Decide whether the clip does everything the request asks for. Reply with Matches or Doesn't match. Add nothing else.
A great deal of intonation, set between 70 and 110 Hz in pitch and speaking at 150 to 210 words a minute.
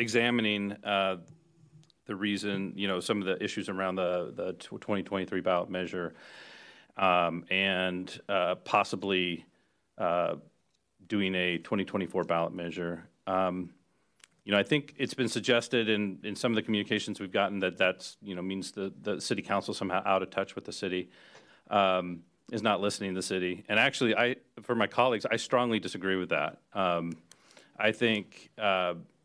Doesn't match